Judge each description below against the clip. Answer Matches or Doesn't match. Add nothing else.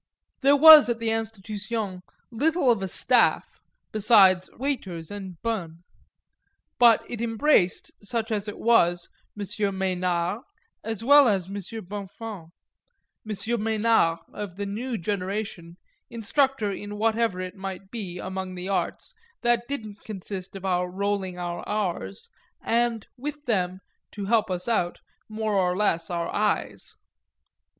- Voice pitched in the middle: Doesn't match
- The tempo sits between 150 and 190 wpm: Doesn't match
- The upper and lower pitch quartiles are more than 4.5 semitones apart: Doesn't match